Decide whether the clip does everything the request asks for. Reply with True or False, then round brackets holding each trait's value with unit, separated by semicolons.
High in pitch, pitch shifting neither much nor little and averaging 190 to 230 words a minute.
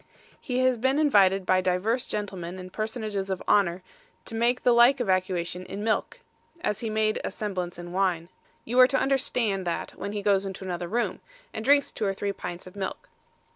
True (200 Hz; 4.2 semitones; 195 wpm)